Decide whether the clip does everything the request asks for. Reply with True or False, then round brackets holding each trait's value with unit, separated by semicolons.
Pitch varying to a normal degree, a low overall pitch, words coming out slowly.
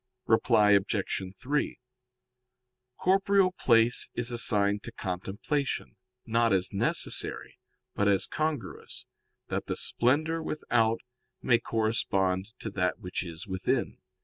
True (4.9 semitones; 110 Hz; 110 wpm)